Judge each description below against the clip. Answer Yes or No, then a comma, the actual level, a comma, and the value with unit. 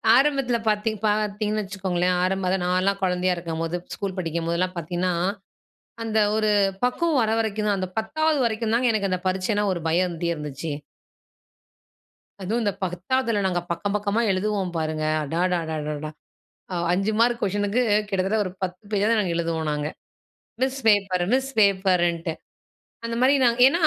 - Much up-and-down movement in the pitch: No, average, 3.7 semitones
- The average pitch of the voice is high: Yes, high, 195 Hz